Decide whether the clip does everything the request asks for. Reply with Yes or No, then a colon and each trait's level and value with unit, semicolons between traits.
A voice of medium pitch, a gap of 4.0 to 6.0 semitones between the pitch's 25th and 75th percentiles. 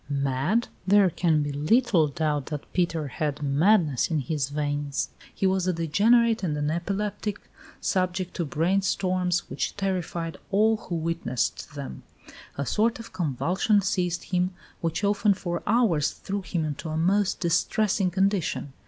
Yes: medium, 175 Hz; average, 4.5 semitones